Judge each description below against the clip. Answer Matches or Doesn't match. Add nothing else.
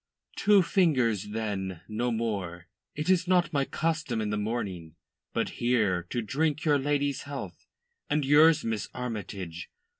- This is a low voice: Matches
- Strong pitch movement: Matches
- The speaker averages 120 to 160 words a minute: Matches